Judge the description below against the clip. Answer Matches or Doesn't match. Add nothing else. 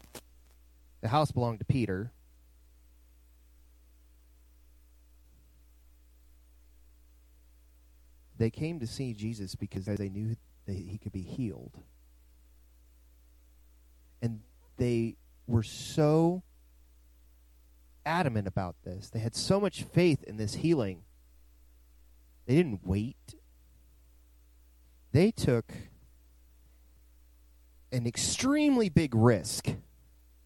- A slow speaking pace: Matches